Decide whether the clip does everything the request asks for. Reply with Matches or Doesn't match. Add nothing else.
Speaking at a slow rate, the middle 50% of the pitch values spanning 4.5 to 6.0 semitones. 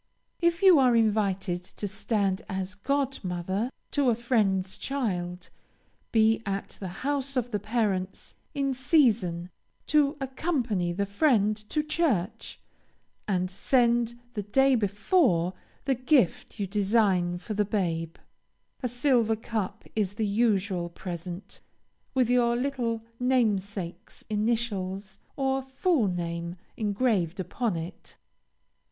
Matches